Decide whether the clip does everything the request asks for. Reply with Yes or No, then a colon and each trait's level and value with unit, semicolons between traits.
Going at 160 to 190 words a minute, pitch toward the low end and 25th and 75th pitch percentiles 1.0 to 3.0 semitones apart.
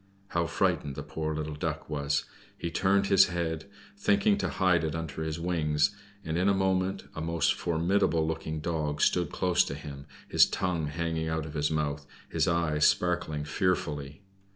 Yes: average, 175 wpm; very low, 80 Hz; average, 2.7 semitones